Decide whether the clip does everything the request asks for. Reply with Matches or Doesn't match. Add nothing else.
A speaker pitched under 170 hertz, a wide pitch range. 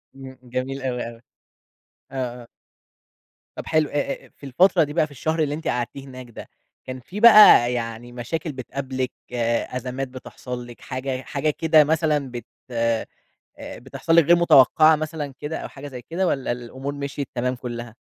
Doesn't match